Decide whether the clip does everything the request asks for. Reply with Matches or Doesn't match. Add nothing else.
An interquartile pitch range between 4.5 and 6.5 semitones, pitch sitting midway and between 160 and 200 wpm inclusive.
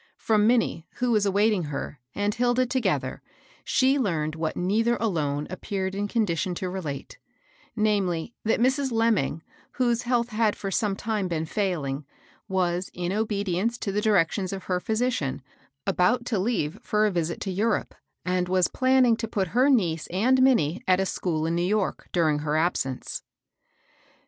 Doesn't match